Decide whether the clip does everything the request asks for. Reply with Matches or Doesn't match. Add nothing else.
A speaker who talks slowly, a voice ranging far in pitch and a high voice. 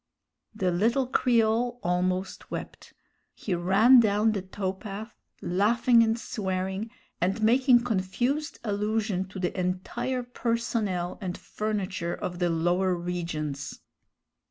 Doesn't match